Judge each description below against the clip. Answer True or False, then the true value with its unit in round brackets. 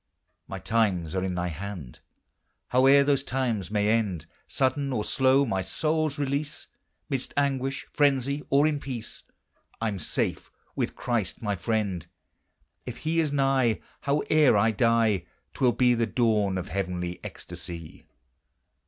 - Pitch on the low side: True (115 Hz)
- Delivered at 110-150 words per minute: True (140 wpm)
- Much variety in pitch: True (5.9 semitones)